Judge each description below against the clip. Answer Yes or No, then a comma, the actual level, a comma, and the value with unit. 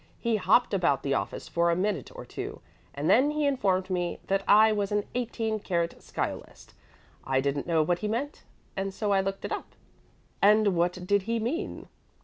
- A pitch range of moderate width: Yes, average, 4.1 semitones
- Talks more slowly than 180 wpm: No, average, 190 wpm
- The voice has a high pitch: Yes, high, 195 Hz